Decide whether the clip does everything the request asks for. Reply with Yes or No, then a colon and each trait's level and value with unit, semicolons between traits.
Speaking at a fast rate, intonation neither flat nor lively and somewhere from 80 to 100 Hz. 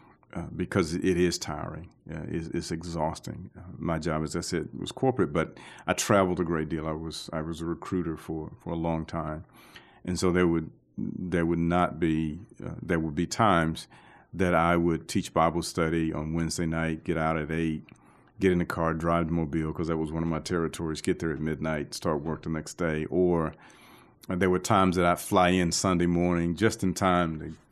No: fast, 210 wpm; narrow, 1.9 semitones; very low, 85 Hz